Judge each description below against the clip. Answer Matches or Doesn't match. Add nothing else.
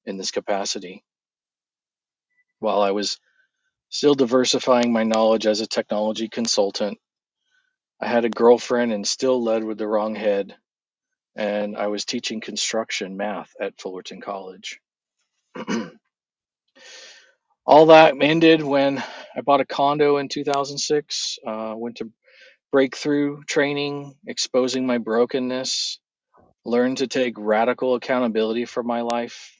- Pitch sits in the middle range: Doesn't match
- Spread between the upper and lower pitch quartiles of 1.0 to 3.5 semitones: Doesn't match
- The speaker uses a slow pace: Matches